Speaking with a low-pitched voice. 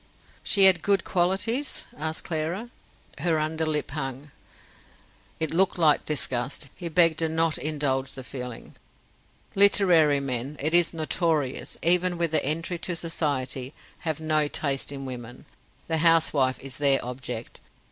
No: medium, 155 Hz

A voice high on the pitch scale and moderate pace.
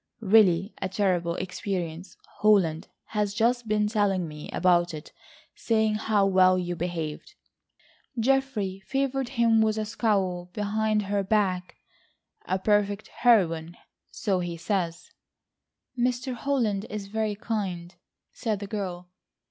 No: high, 205 Hz; slow, 115 wpm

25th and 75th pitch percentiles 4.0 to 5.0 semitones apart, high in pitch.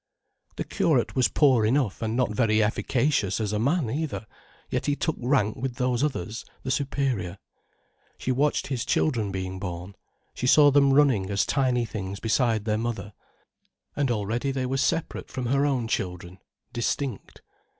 No: average, 4.4 semitones; low, 120 Hz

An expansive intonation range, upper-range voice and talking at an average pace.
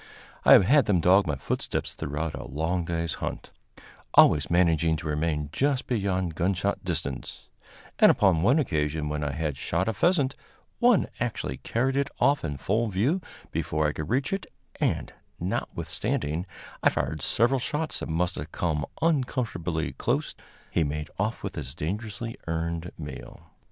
No: wide, 7.1 semitones; very low, 85 Hz; average, 160 wpm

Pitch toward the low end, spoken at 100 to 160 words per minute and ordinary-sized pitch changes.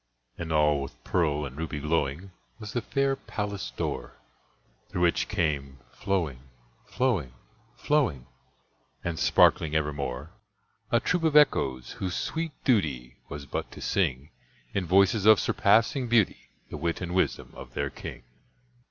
No: very low, 85 Hz; average, 140 wpm; wide, 6.8 semitones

